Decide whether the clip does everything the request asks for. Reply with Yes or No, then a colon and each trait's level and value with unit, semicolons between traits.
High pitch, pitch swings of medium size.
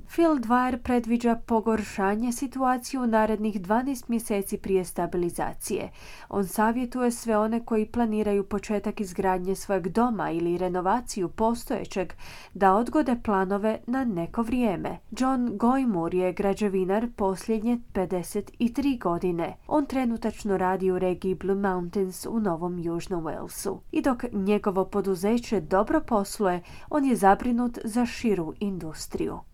Yes: high, 210 Hz; average, 4.0 semitones